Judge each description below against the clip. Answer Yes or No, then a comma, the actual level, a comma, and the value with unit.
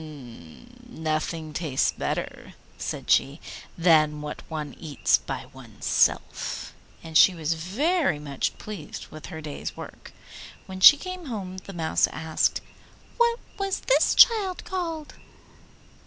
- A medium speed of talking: No, slow, 125 wpm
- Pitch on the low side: No, medium, 170 Hz